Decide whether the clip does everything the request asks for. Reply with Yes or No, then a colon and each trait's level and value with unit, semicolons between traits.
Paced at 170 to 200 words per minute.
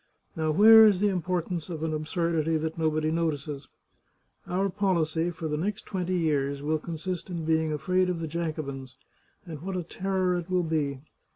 Yes: average, 175 wpm